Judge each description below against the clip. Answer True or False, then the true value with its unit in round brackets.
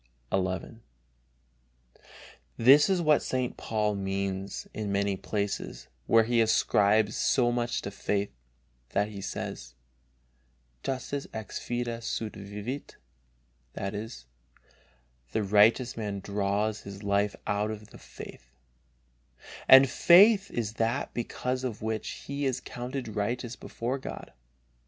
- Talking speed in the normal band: False (115 wpm)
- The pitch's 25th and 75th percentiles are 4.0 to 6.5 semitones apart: False (3.5 semitones)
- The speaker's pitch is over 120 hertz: False (110 Hz)